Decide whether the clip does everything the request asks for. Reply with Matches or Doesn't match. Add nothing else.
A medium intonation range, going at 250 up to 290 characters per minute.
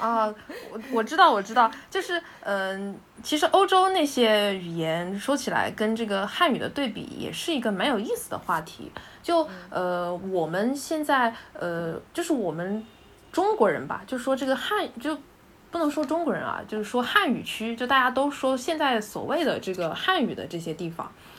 Doesn't match